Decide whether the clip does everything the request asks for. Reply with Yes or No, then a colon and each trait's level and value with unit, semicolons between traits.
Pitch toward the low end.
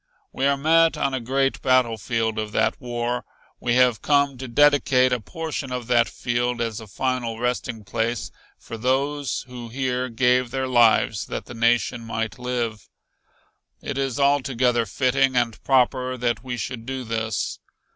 Yes: low, 125 Hz